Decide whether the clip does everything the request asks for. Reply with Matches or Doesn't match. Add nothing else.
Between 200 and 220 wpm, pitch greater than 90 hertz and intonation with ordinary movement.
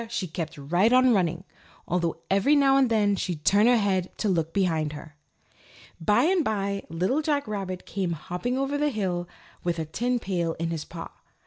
Doesn't match